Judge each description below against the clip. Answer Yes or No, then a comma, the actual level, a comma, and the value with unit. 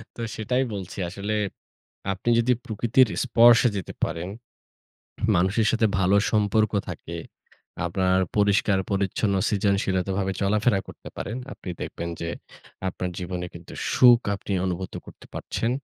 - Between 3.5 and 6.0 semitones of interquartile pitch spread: No, average, 3.1 semitones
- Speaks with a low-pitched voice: Yes, low, 100 Hz